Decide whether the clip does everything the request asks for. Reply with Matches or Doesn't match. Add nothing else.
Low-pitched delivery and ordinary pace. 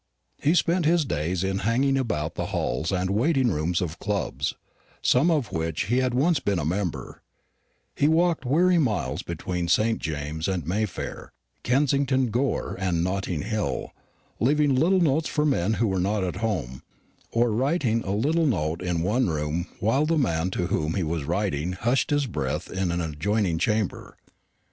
Matches